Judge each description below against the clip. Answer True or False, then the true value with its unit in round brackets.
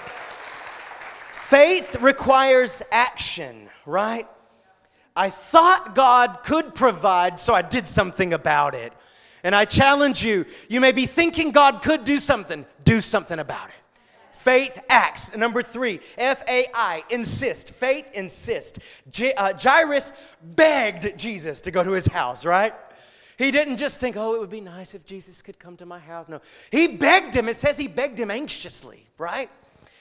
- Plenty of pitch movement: True (6.3 semitones)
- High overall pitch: True (245 Hz)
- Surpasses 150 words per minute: True (160 wpm)